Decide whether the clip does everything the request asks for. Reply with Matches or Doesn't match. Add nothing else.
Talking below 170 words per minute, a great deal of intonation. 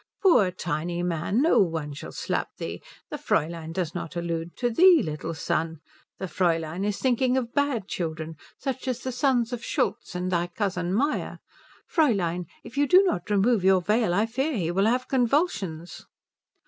Doesn't match